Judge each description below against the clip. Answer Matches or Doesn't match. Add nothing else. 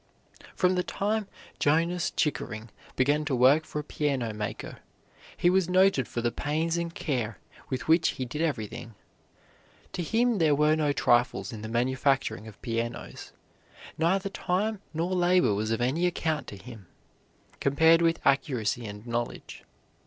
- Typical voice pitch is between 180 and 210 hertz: Doesn't match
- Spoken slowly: Doesn't match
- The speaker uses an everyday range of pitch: Doesn't match